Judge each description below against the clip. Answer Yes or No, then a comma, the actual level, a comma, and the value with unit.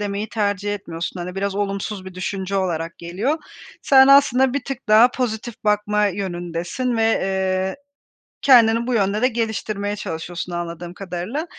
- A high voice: Yes, high, 205 Hz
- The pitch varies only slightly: No, average, 3.7 semitones